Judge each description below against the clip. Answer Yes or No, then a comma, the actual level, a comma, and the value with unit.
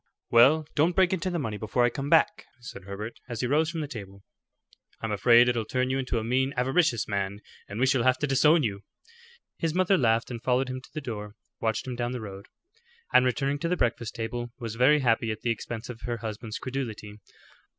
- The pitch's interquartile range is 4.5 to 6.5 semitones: No, average, 3.5 semitones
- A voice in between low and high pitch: No, low, 120 Hz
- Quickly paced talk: Yes, fast, 220 wpm